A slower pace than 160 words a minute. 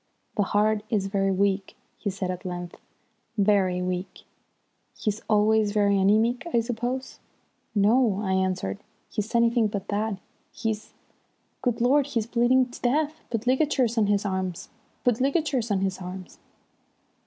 Yes: average, 145 wpm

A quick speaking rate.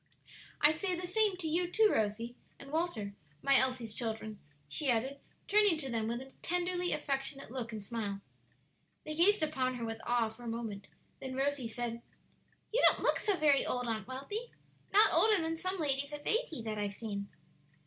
No: average, 185 wpm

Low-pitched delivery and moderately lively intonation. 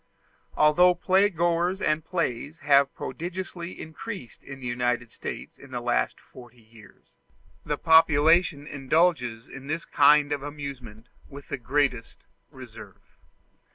No: medium, 145 Hz; average, 5.0 semitones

